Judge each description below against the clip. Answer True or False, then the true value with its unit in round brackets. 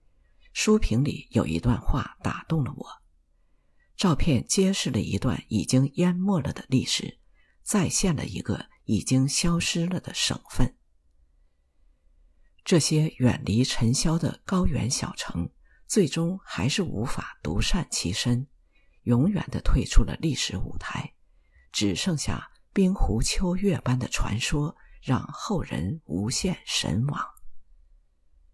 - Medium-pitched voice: False (120 Hz)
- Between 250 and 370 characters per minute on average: False (185 characters per minute)